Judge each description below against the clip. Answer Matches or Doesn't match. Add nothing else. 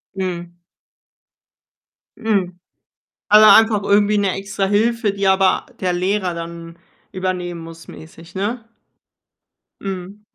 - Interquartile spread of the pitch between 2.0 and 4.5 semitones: Matches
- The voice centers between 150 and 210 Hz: Matches